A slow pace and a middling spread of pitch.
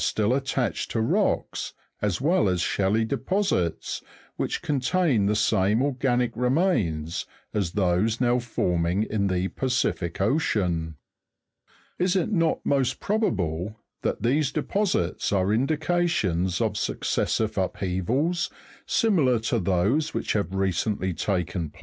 No: slow, 125 wpm; wide, 7.0 semitones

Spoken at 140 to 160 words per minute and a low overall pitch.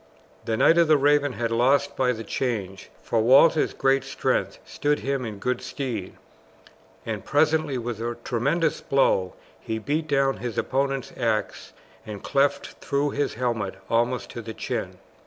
Yes: average, 155 wpm; low, 125 Hz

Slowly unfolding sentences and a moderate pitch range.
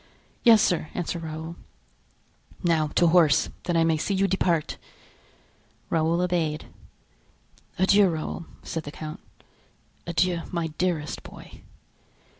No: slow, 115 wpm; narrow, 2.2 semitones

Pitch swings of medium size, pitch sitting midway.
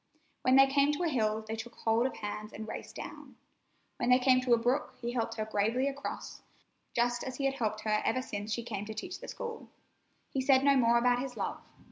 No: average, 3.4 semitones; high, 240 Hz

